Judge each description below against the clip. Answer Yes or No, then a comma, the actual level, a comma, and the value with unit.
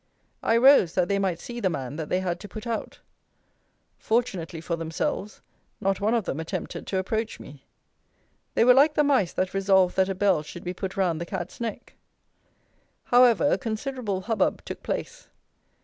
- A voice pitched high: Yes, high, 195 Hz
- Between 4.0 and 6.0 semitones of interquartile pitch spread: Yes, average, 4.6 semitones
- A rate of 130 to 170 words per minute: No, average, 180 wpm